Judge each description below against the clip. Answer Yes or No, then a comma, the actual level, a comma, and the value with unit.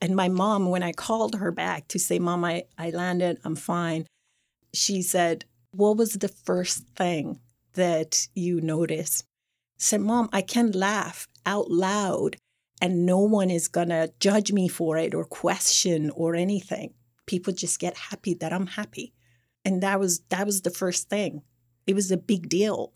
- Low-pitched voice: No, medium, 180 Hz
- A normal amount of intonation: Yes, average, 3.3 semitones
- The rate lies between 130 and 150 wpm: No, average, 175 wpm